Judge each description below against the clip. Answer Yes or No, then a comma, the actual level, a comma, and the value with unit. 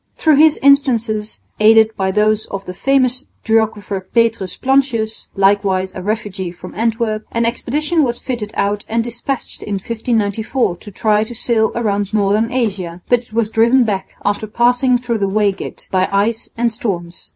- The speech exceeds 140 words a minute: Yes, average, 160 wpm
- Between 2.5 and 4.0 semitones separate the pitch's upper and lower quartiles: Yes, average, 2.9 semitones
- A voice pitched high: Yes, high, 220 Hz